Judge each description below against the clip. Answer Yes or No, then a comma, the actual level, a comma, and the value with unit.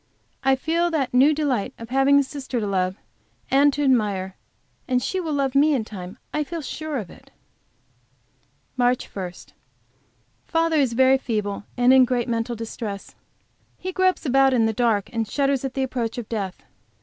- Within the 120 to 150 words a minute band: No, average, 175 wpm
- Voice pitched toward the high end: Yes, very high, 255 Hz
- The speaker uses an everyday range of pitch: Yes, average, 4.0 semitones